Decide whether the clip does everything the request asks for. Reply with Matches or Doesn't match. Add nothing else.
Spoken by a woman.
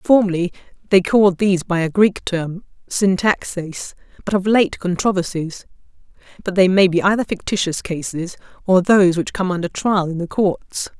Matches